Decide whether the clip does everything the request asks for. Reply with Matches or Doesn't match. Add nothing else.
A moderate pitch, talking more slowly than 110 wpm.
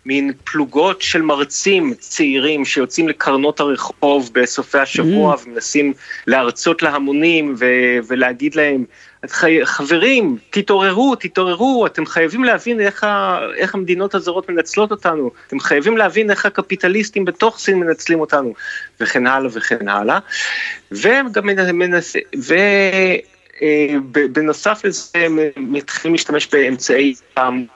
Matches